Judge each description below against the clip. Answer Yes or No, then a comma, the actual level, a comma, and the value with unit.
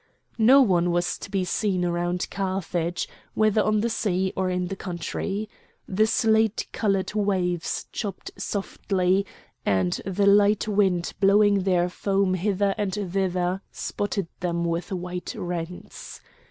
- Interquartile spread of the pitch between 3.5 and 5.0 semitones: No, narrow, 2.4 semitones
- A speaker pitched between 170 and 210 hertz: Yes, high, 190 Hz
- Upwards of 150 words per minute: No, slow, 135 wpm